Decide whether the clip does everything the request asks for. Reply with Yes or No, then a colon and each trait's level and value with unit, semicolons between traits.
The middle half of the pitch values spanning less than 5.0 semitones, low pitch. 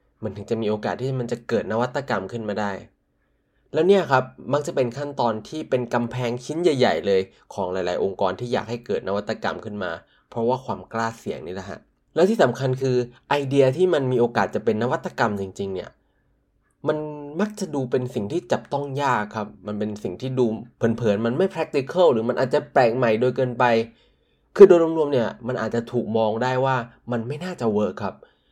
Yes: average, 3.8 semitones; low, 125 Hz